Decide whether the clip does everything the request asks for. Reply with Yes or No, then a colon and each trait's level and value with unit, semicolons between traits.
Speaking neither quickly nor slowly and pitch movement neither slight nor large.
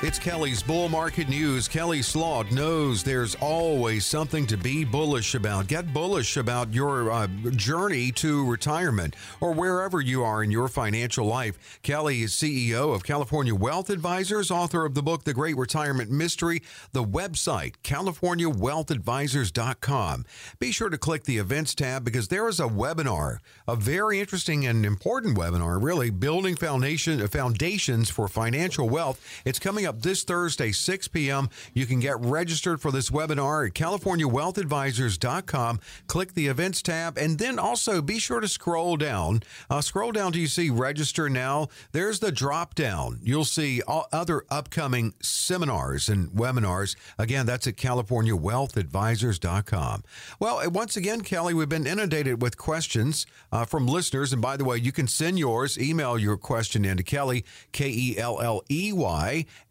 No: average, 155 wpm; wide, 5.7 semitones